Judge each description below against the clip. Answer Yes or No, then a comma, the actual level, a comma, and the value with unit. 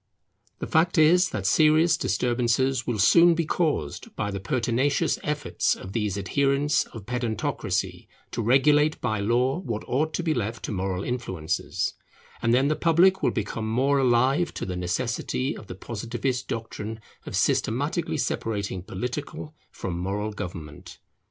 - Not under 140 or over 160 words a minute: Yes, average, 150 wpm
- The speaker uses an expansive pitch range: Yes, wide, 6.0 semitones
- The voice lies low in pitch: Yes, low, 120 Hz